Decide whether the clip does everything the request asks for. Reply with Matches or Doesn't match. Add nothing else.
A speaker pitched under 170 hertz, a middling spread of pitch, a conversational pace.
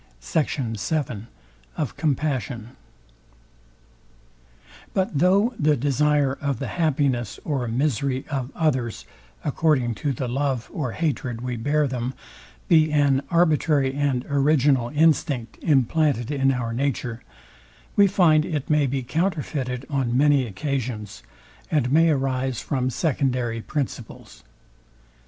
Doesn't match